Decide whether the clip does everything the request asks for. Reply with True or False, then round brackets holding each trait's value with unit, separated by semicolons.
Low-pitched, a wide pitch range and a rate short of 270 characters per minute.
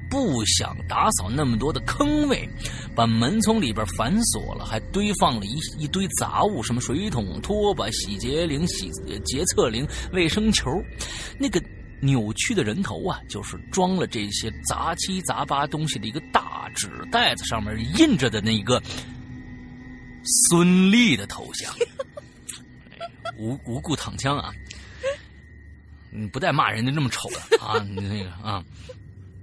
True (125 Hz; 8.8 semitones; 210 characters per minute)